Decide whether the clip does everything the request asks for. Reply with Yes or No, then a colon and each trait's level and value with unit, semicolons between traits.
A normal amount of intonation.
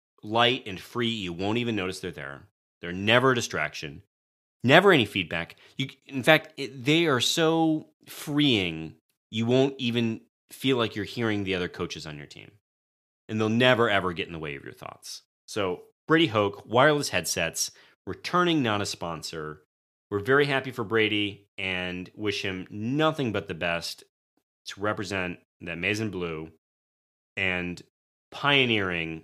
No: wide, 6.4 semitones